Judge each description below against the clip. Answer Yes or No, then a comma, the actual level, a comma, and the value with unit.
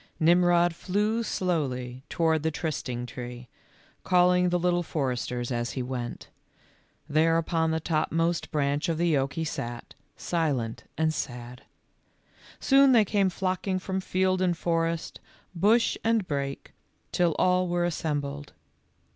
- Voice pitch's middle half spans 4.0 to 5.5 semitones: Yes, average, 4.5 semitones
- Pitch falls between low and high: Yes, medium, 165 Hz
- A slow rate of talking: Yes, slow, 130 wpm